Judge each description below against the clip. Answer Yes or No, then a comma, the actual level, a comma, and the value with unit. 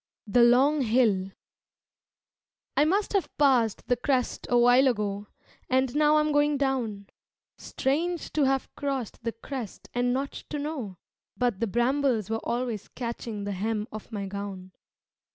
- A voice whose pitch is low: No, high, 245 Hz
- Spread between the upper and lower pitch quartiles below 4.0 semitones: No, average, 4.3 semitones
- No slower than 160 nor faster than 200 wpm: No, average, 150 wpm